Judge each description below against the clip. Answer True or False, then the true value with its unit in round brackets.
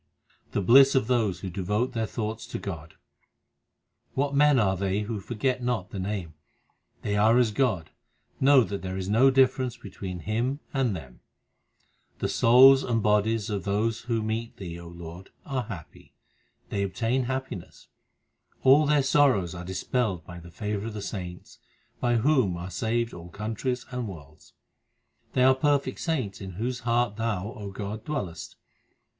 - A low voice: True (110 Hz)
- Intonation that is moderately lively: True (4.8 semitones)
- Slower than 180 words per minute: True (165 wpm)